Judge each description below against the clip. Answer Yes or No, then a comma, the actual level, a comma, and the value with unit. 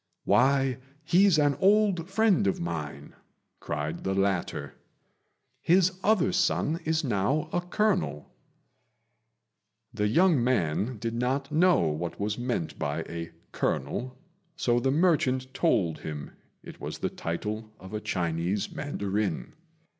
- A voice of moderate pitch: No, low, 120 Hz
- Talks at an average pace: No, slow, 125 wpm